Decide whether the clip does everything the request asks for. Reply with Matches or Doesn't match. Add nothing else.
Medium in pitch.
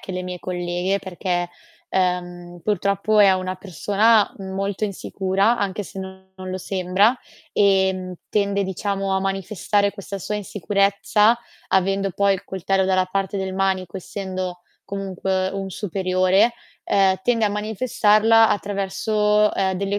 Doesn't match